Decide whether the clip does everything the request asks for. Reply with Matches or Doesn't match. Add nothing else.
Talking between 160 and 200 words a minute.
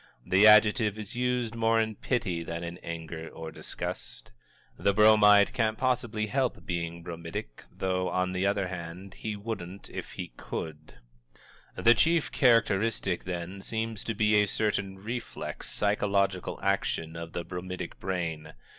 Doesn't match